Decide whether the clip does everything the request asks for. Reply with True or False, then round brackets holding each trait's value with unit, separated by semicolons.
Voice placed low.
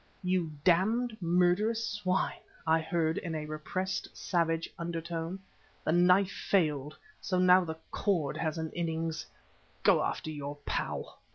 False (170 Hz)